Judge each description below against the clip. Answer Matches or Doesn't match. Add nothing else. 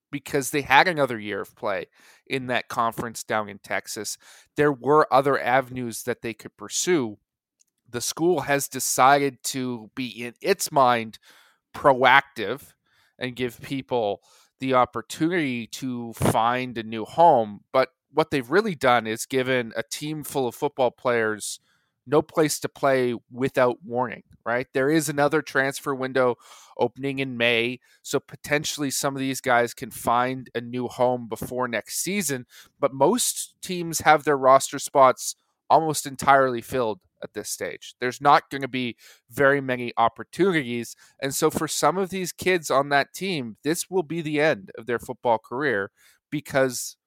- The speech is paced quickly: Doesn't match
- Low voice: Matches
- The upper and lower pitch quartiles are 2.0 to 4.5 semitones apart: Matches